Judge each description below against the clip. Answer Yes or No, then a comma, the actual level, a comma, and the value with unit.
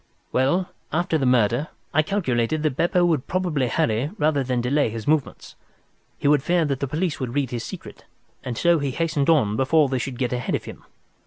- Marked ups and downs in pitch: No, average, 4.2 semitones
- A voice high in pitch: No, medium, 140 Hz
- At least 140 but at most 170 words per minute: No, average, 200 wpm